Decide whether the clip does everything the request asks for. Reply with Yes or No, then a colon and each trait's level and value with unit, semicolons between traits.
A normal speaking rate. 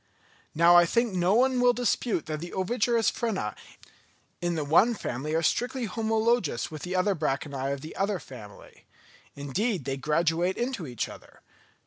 Yes: average, 155 wpm